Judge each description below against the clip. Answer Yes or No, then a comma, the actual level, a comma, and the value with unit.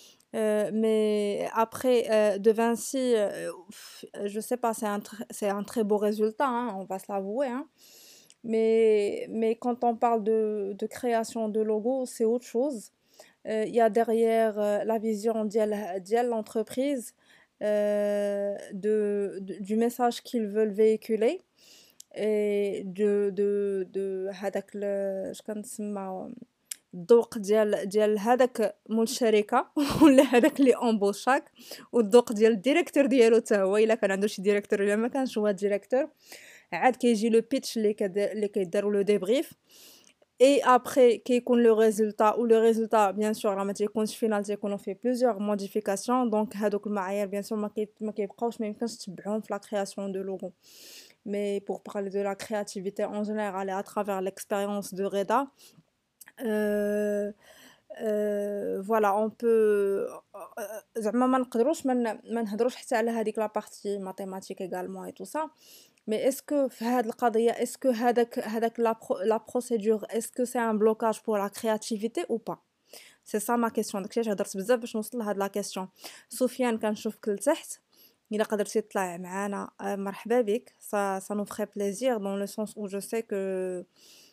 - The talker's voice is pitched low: No, high, 215 Hz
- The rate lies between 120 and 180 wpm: Yes, fast, 135 wpm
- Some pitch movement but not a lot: No, narrow, 2.3 semitones